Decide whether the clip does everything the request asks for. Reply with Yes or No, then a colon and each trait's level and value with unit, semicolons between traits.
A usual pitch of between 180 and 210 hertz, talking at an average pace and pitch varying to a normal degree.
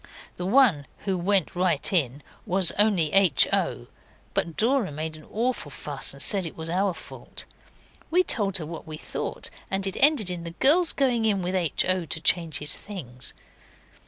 Yes: medium, 185 Hz; average, 185 wpm; average, 4.4 semitones